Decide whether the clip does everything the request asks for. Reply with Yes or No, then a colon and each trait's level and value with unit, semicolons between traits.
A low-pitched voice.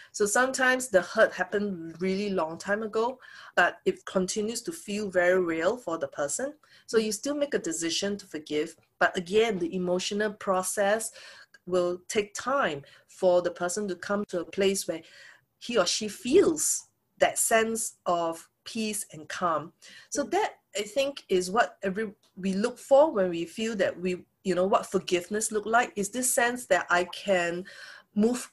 No: high, 200 Hz